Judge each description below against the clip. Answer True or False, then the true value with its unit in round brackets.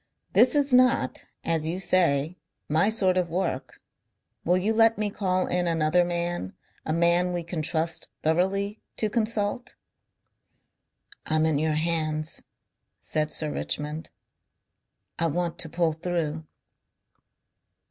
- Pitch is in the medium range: True (170 Hz)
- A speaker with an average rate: False (125 wpm)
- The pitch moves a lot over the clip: False (2.9 semitones)